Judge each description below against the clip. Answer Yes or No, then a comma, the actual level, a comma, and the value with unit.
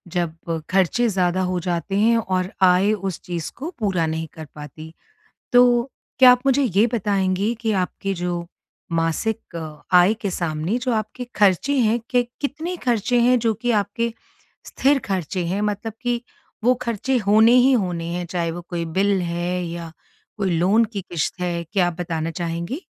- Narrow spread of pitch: No, average, 5.0 semitones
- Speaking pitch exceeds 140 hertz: Yes, high, 190 Hz